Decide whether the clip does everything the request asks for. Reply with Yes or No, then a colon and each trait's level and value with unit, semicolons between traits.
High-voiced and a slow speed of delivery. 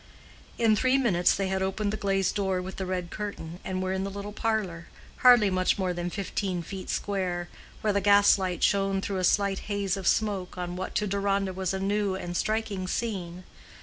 No: high, 195 Hz; average, 200 wpm